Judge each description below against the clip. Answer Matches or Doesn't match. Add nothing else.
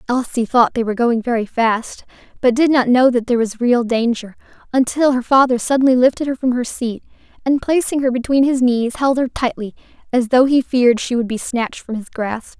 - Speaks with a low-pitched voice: Doesn't match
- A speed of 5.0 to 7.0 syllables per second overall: Matches